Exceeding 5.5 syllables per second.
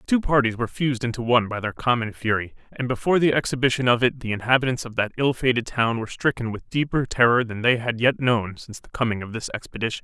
Yes: 6.7 syllables/s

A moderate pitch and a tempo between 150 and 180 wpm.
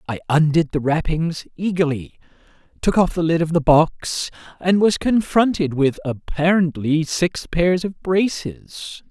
No: medium, 165 Hz; average, 140 wpm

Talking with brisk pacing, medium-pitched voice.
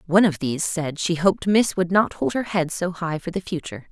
Yes: fast, 260 wpm; medium, 175 Hz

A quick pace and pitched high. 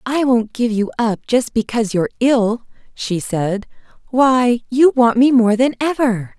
No: average, 170 wpm; high, 235 Hz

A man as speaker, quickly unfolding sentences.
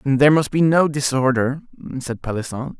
No: male; average, 150 wpm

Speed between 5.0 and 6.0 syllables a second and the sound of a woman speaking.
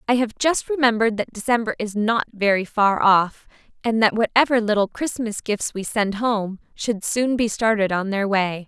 No: 4.8 syllables/s; female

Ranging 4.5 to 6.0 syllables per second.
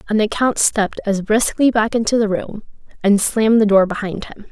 Yes: 5.5 syllables/s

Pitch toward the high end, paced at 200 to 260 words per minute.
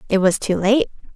Yes: high, 215 Hz; fast, 205 wpm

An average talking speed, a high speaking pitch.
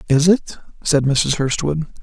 No: average, 150 wpm; medium, 150 Hz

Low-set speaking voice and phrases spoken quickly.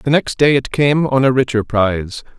Yes: low, 130 Hz; fast, 225 wpm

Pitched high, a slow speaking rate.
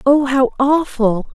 Yes: very high, 270 Hz; slow, 130 wpm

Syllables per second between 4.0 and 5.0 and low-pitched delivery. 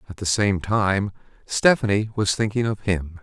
Yes: 4.5 syllables/s; low, 100 Hz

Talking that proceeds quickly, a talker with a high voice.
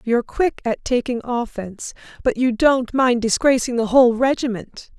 No: average, 155 wpm; high, 240 Hz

